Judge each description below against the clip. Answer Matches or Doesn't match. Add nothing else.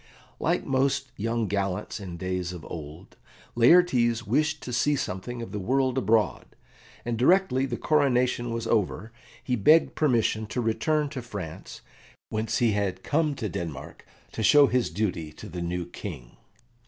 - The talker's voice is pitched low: Matches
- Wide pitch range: Matches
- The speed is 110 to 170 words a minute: Matches